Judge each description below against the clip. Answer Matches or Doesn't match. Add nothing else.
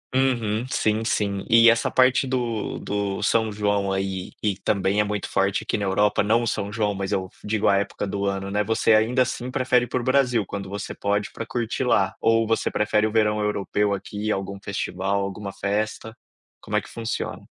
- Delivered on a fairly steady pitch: Matches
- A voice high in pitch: Doesn't match